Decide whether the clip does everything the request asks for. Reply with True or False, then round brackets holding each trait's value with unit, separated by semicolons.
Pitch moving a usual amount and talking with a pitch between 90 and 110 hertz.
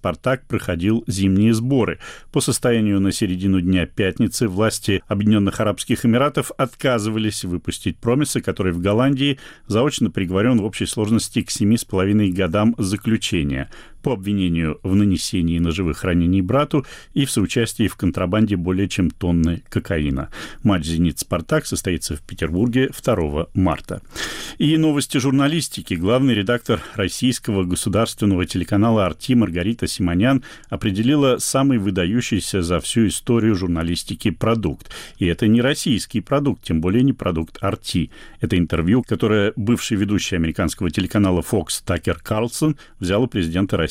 True (4.6 semitones; 105 Hz)